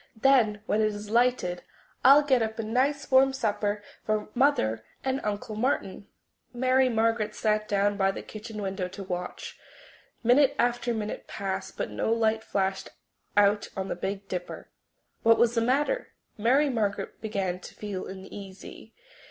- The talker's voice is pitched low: No, high, 215 Hz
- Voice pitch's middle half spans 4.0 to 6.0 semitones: No, average, 3.5 semitones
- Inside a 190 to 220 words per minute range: No, average, 155 wpm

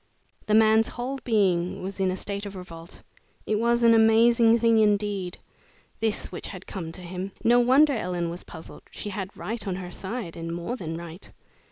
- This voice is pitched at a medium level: No, high, 200 Hz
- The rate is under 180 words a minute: No, average, 190 wpm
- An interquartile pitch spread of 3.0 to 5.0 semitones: Yes, average, 4.0 semitones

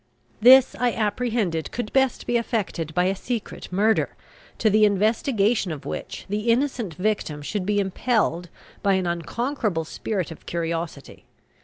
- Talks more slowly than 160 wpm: Yes, average, 145 wpm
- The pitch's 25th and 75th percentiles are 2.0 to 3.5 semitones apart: No, average, 5.0 semitones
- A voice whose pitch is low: No, high, 205 Hz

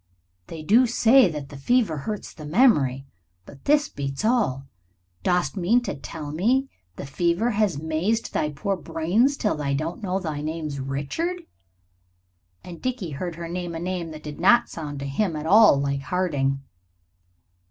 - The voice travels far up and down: Yes, wide, 6.9 semitones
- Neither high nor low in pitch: Yes, medium, 165 Hz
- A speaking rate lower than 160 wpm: No, average, 175 wpm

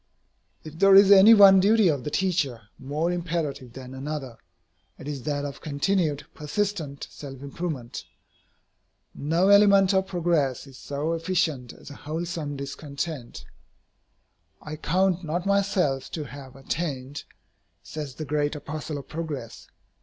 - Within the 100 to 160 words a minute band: Yes, slow, 135 wpm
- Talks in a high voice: No, medium, 155 Hz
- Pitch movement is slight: No, average, 4.2 semitones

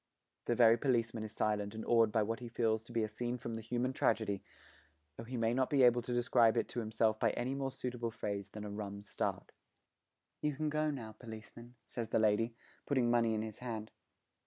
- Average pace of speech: No, fast, 215 wpm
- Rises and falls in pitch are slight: Yes, narrow, 2.0 semitones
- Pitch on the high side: No, low, 115 Hz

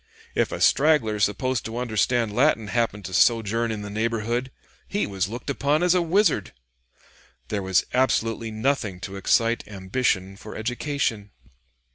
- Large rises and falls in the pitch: No, average, 3.8 semitones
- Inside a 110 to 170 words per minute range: Yes, average, 145 wpm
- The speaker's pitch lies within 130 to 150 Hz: No, low, 115 Hz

